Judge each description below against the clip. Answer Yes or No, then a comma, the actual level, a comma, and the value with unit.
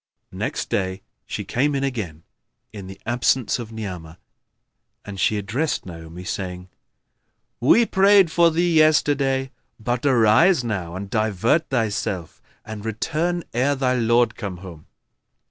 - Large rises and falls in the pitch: Yes, wide, 6.5 semitones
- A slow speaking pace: Yes, slow, 130 wpm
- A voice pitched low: Yes, low, 115 Hz